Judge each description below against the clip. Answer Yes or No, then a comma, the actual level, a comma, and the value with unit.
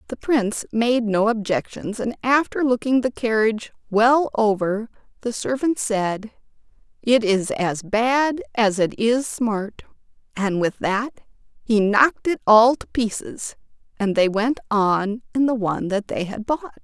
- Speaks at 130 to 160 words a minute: Yes, average, 155 wpm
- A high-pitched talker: Yes, high, 225 Hz